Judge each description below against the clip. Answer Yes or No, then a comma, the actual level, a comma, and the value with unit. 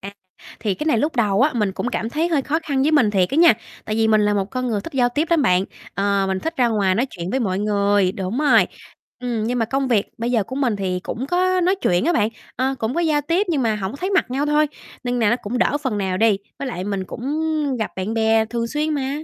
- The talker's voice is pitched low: No, high, 235 Hz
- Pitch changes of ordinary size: No, wide, 5.8 semitones